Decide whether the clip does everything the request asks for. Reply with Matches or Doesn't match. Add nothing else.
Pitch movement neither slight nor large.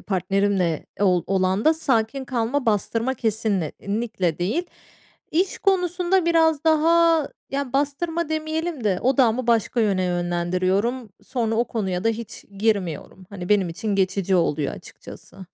Doesn't match